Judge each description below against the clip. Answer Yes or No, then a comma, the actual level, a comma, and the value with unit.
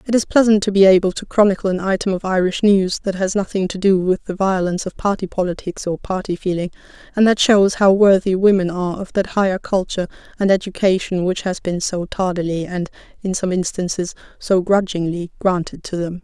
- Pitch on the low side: No, high, 190 Hz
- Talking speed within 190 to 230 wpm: Yes, average, 200 wpm